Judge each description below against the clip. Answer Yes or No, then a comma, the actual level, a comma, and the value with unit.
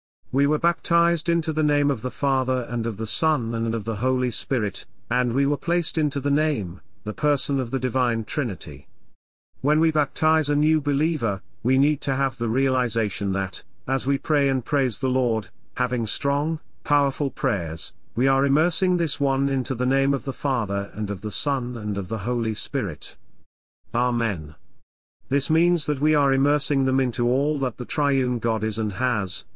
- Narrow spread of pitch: No, average, 4.3 semitones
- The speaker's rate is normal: Yes, average, 185 wpm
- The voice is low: Yes, low, 130 Hz